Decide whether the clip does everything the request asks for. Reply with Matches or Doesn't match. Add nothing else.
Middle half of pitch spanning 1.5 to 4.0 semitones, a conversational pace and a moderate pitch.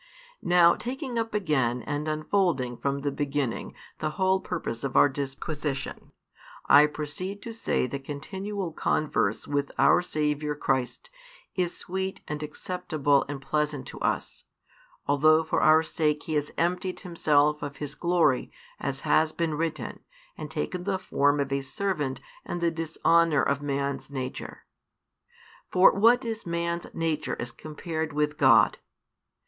Matches